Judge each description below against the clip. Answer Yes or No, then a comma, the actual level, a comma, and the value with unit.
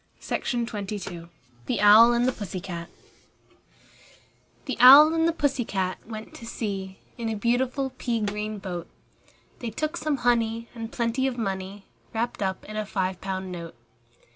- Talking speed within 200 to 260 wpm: No, average, 160 wpm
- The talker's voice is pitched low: No, high, 220 Hz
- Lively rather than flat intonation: No, average, 4.0 semitones